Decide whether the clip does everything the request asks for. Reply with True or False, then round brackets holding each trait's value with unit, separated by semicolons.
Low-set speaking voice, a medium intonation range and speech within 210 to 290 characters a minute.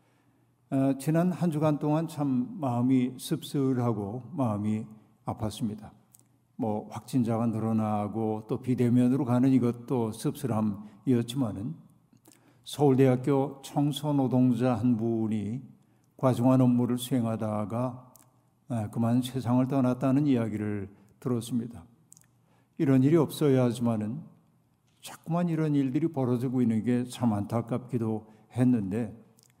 True (125 Hz; 3.0 semitones; 260 characters per minute)